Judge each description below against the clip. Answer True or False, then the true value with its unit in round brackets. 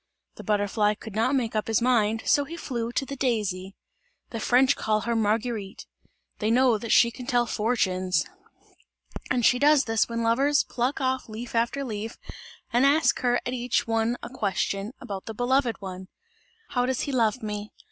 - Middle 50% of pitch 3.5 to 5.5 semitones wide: False (3.0 semitones)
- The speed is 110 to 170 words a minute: False (180 wpm)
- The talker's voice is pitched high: True (230 Hz)